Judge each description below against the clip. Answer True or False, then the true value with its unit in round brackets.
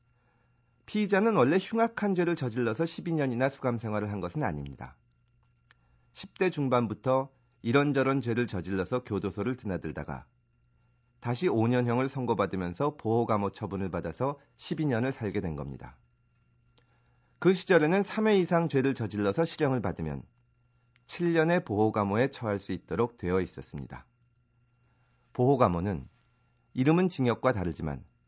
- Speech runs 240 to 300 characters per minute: True (295 characters per minute)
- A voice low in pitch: True (125 Hz)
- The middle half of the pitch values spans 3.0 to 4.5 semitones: False (5.4 semitones)